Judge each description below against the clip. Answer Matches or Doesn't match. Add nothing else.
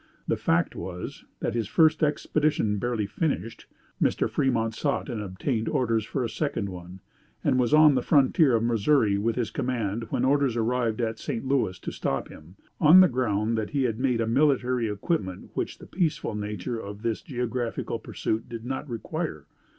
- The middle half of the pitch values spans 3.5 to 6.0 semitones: Matches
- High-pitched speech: Doesn't match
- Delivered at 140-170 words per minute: Doesn't match